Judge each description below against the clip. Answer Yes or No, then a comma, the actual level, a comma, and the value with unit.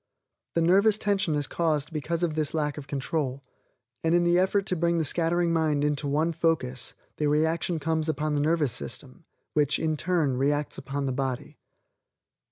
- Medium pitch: Yes, medium, 155 Hz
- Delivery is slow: No, average, 175 wpm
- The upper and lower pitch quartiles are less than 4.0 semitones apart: Yes, average, 2.7 semitones